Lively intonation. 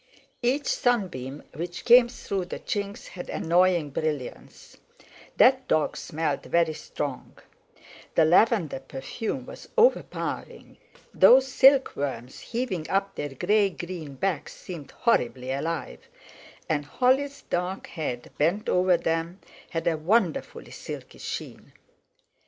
Yes: wide, 6.7 semitones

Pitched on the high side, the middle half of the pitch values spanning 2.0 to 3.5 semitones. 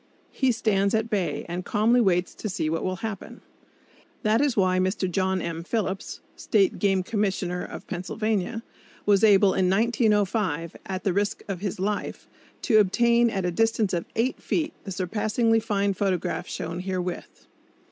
Yes: high, 200 Hz; average, 3.2 semitones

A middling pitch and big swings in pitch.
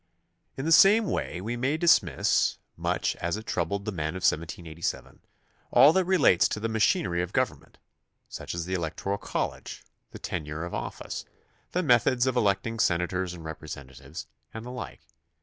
No: very low, 95 Hz; wide, 6.4 semitones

